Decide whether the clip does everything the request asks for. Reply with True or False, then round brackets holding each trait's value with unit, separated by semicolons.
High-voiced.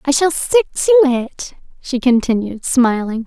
True (265 Hz)